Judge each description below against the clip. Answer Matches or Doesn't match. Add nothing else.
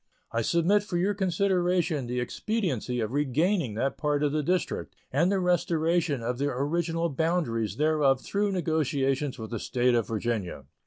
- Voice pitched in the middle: Matches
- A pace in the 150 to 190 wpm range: Matches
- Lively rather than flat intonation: Matches